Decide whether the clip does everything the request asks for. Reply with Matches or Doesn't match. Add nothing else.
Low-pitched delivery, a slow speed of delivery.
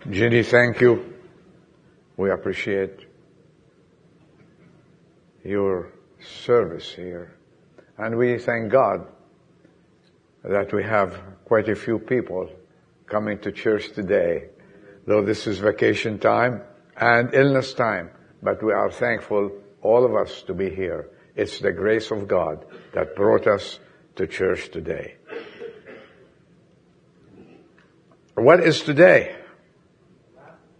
Matches